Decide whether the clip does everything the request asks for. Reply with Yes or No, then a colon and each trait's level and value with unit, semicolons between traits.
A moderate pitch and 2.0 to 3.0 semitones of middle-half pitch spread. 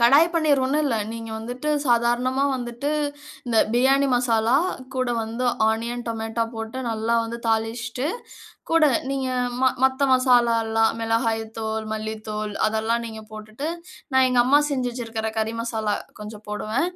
No: high, 235 Hz; narrow, 2.6 semitones